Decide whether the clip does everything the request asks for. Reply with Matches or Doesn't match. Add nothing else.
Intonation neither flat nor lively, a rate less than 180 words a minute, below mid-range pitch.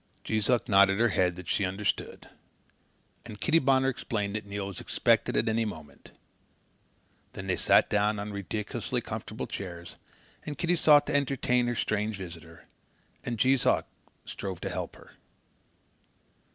Matches